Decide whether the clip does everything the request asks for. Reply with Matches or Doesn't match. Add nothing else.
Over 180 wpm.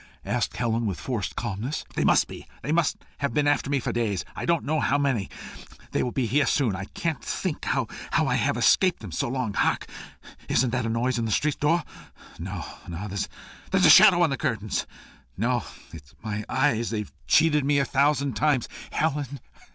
Matches